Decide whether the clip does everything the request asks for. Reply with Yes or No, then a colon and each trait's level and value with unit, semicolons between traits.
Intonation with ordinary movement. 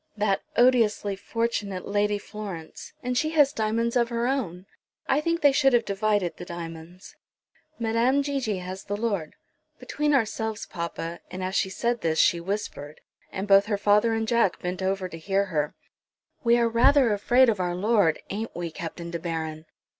Yes: average, 4.6 semitones